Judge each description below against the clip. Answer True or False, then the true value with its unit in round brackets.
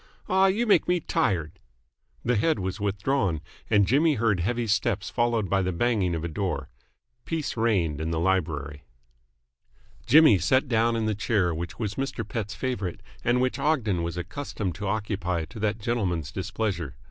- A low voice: True (105 Hz)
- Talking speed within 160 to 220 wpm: True (170 wpm)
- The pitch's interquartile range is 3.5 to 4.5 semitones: False (5.4 semitones)